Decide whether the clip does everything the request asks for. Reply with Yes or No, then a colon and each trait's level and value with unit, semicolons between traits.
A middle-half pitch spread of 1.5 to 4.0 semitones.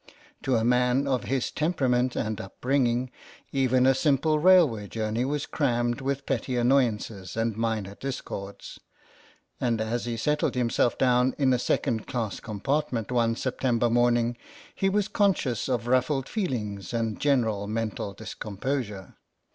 Yes: average, 3.1 semitones